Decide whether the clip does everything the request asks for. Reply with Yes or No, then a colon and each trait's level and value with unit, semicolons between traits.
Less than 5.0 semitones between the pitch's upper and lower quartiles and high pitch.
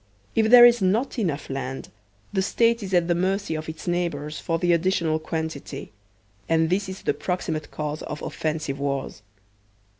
No: average, 3.8 semitones; medium, 165 Hz